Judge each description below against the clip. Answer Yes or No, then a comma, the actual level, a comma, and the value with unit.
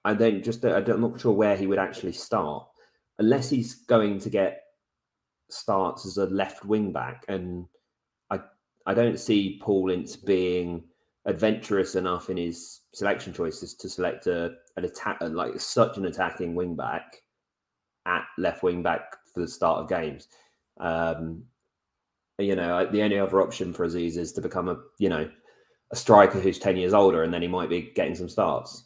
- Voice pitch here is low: Yes, very low, 95 Hz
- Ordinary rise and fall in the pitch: Yes, average, 3.1 semitones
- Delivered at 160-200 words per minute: Yes, average, 180 wpm